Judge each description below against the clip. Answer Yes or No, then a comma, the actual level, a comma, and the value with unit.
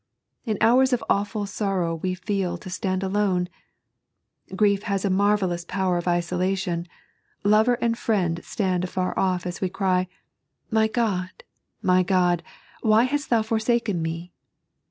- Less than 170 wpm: Yes, average, 150 wpm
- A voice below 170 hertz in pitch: No, high, 190 Hz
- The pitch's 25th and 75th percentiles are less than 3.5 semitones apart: Yes, average, 3.0 semitones